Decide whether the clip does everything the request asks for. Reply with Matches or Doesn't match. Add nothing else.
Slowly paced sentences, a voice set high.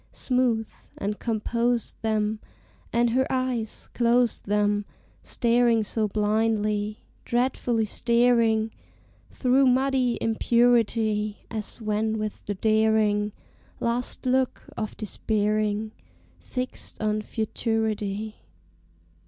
Matches